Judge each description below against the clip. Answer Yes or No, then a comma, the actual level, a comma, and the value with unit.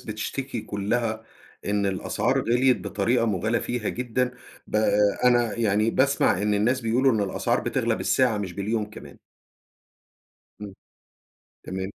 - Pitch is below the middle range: Yes, low, 110 Hz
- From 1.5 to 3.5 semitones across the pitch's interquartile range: Yes, average, 3.1 semitones